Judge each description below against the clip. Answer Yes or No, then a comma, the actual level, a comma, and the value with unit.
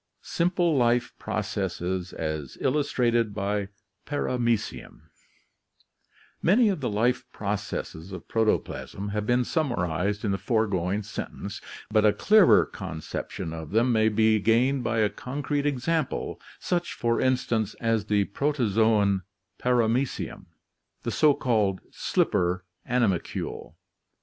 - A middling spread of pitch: Yes, average, 4.0 semitones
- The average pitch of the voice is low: Yes, low, 110 Hz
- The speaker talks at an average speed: No, slow, 115 wpm